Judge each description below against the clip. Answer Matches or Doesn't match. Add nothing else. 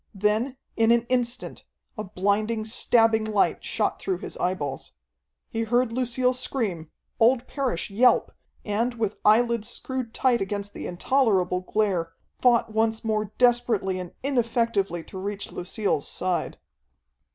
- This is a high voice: Matches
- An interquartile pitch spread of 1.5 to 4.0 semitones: Matches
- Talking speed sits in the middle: Doesn't match